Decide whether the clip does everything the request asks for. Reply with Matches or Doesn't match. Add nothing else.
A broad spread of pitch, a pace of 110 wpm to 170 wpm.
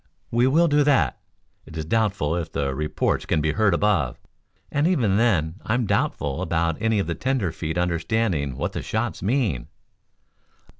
Matches